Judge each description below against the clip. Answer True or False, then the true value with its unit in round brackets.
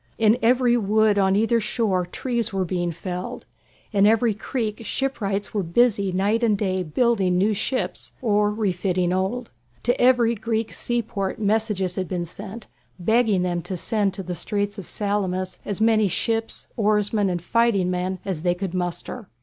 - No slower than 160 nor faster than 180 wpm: True (165 wpm)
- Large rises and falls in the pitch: False (3.3 semitones)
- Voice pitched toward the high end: True (205 Hz)